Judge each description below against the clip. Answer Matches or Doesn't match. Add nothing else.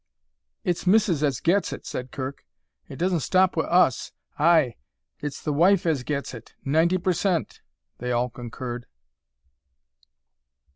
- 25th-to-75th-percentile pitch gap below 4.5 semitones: Doesn't match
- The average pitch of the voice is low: Doesn't match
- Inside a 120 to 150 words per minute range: Matches